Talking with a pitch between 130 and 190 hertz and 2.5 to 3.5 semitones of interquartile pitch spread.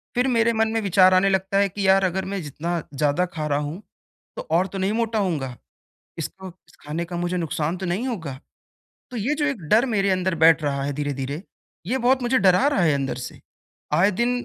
No: medium, 185 Hz; average, 4.9 semitones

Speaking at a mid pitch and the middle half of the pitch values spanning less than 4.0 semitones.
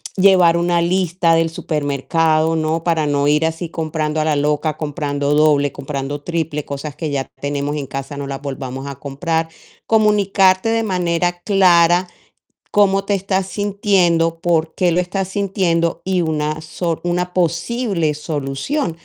Yes: medium, 165 Hz; average, 3.4 semitones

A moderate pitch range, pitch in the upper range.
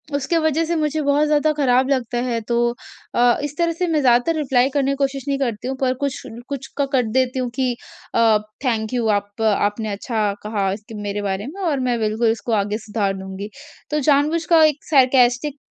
Yes: average, 4.4 semitones; very high, 255 Hz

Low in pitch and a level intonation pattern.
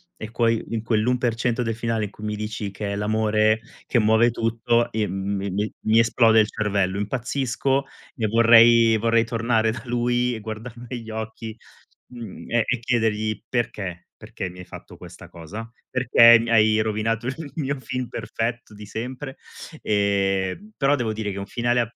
Yes: low, 115 Hz; narrow, 1.9 semitones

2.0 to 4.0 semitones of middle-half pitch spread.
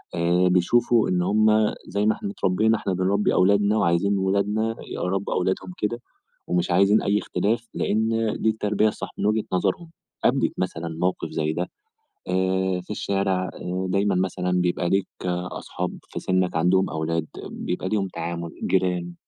Yes: average, 2.8 semitones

